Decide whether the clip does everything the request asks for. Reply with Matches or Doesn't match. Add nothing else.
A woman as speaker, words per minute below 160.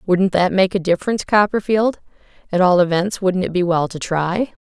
Doesn't match